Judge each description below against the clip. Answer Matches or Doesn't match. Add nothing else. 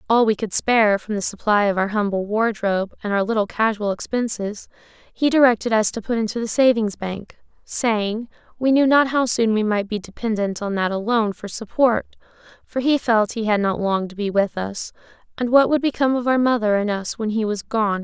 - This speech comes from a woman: Matches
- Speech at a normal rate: Doesn't match